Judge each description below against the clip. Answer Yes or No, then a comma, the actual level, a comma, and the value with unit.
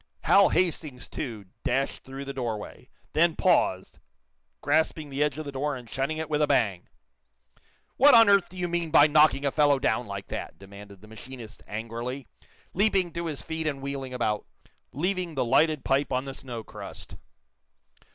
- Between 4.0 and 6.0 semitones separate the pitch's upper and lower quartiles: Yes, average, 4.5 semitones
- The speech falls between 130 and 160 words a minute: No, average, 175 wpm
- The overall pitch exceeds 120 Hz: Yes, medium, 140 Hz